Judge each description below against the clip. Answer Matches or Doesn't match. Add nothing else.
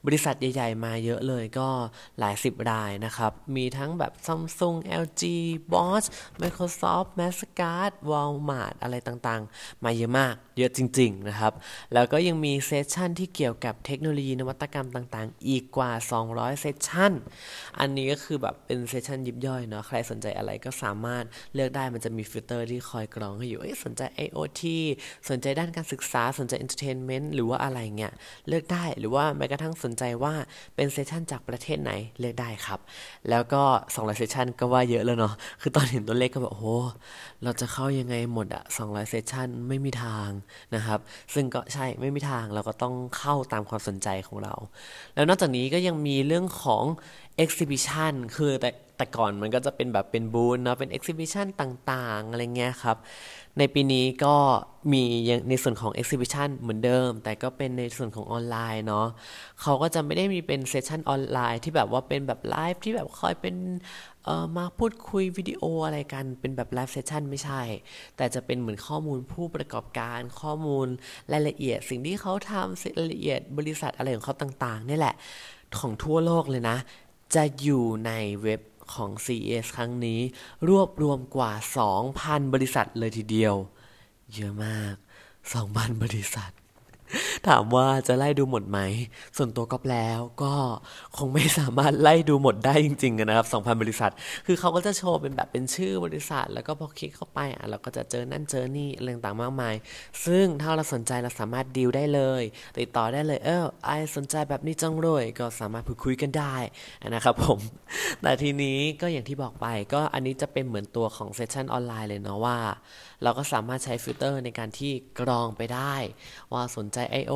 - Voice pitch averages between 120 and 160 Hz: Matches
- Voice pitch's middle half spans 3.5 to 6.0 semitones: Matches